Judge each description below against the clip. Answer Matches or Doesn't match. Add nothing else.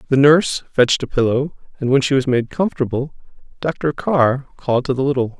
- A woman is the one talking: Doesn't match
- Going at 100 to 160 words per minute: Doesn't match